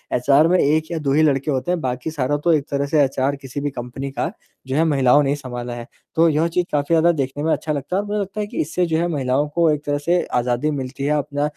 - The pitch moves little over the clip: No, average, 3.0 semitones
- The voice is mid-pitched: Yes, medium, 145 Hz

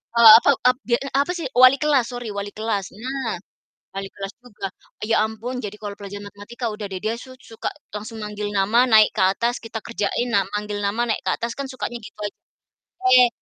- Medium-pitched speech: No, high, 220 Hz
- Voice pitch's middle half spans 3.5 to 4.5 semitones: No, average, 3.0 semitones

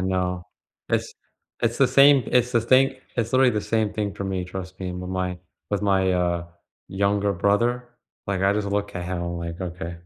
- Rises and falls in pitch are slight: No, average, 3.9 semitones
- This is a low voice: Yes, low, 100 Hz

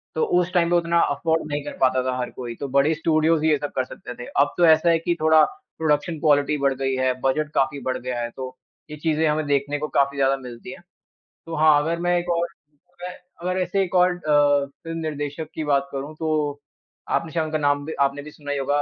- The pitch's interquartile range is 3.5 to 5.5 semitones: No, average, 2.9 semitones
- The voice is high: No, medium, 150 Hz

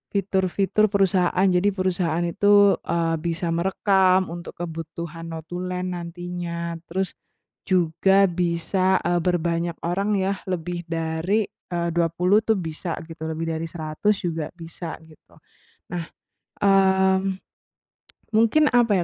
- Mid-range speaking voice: Yes, medium, 175 Hz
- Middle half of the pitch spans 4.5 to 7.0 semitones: No, narrow, 2.4 semitones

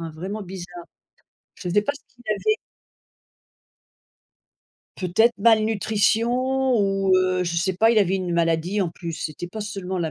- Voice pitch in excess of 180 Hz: Yes, high, 190 Hz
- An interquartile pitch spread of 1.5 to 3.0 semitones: No, average, 3.4 semitones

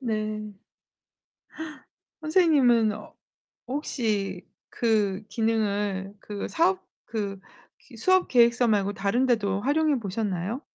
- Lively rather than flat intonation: No, average, 3.9 semitones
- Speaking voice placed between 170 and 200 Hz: No, high, 220 Hz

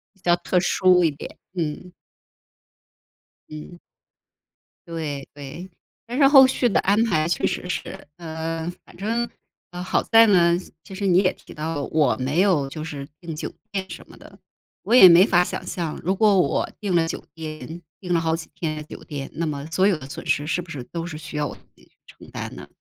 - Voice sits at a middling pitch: Yes, medium, 170 Hz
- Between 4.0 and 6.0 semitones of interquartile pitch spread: No, average, 3.4 semitones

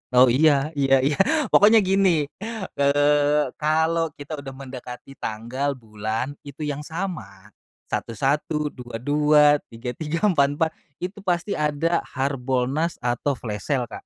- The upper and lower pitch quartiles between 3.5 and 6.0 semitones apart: Yes, average, 4.0 semitones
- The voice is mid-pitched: Yes, medium, 145 Hz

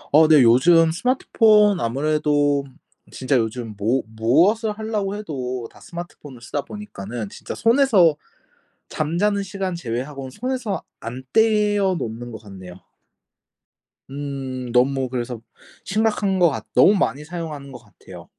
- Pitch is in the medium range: Yes, medium, 150 Hz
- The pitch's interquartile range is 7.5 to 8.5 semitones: Yes, wide, 8.1 semitones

